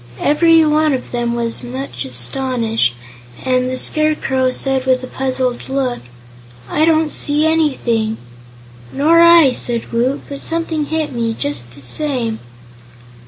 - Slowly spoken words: Yes, slow, 130 wpm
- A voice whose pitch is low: No, very high, 260 Hz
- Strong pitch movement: No, average, 4.7 semitones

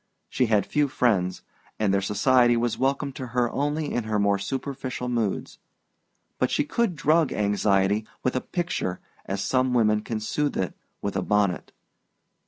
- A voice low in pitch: Yes, low, 120 Hz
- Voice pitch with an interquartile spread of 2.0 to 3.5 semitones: No, average, 4.6 semitones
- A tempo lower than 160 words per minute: No, average, 165 wpm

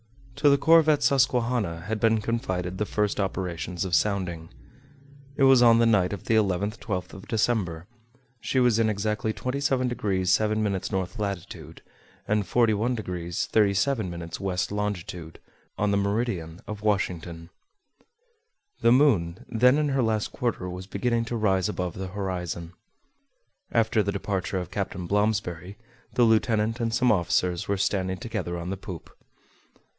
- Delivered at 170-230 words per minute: No, average, 145 wpm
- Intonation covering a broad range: No, average, 4.0 semitones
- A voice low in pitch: Yes, low, 100 Hz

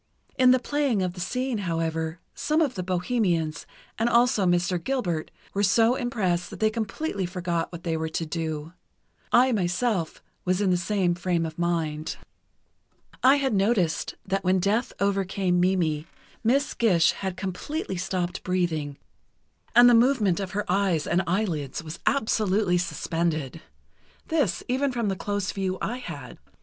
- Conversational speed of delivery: Yes, average, 155 wpm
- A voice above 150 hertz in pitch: Yes, medium, 185 Hz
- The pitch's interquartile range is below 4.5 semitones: No, average, 4.8 semitones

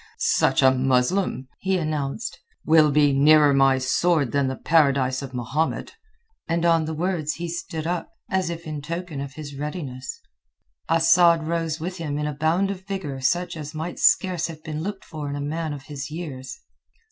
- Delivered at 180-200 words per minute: Yes, average, 185 wpm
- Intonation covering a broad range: No, average, 3.2 semitones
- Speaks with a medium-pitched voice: Yes, medium, 155 Hz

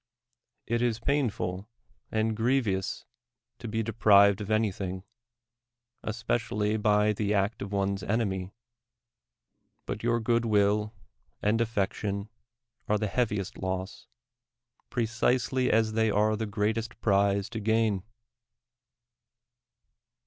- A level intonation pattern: Yes, narrow, 2.1 semitones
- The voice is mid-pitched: No, low, 105 Hz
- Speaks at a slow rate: Yes, slow, 110 wpm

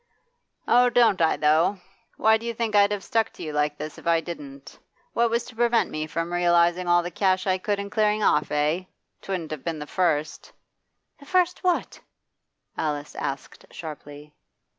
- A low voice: No, medium, 175 Hz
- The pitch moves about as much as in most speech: No, wide, 5.9 semitones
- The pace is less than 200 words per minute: Yes, average, 185 wpm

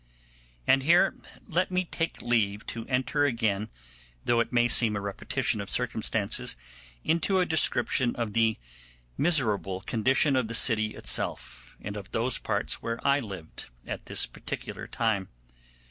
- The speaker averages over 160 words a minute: No, average, 145 wpm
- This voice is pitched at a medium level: No, low, 115 Hz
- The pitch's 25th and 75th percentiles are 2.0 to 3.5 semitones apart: No, average, 4.2 semitones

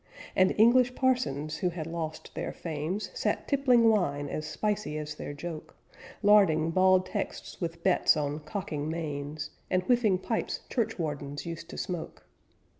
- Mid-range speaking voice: Yes, medium, 170 Hz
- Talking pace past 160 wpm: No, average, 145 wpm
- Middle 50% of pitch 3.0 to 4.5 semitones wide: No, average, 5.2 semitones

